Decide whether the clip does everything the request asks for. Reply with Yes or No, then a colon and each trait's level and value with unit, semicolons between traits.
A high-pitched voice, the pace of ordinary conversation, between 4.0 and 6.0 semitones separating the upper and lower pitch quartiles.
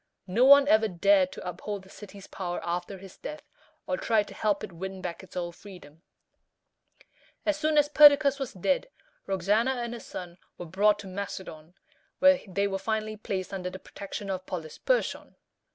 Yes: high, 200 Hz; average, 175 wpm; average, 4.4 semitones